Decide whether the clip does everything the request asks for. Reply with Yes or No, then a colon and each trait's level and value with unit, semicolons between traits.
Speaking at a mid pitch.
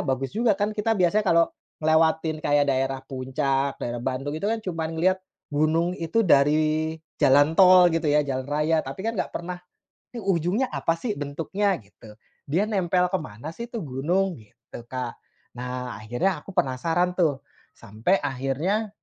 Yes: medium, 160 Hz